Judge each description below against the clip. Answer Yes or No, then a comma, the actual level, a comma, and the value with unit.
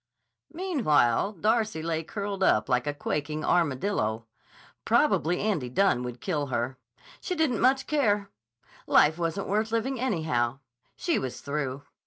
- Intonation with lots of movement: Yes, wide, 8.2 semitones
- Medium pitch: Yes, medium, 165 Hz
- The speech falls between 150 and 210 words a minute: No, slow, 135 wpm